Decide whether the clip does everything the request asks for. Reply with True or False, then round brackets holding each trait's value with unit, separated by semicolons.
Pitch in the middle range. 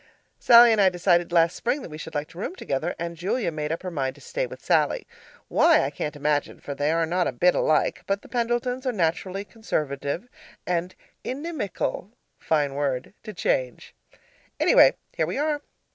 True (175 Hz)